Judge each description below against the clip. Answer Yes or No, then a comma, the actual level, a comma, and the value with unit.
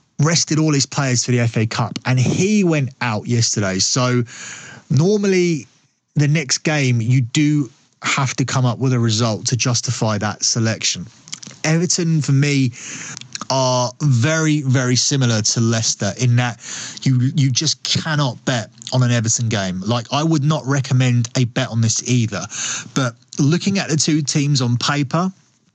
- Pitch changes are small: No, average, 3.7 semitones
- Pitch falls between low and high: No, low, 130 Hz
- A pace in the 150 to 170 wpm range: Yes, average, 160 wpm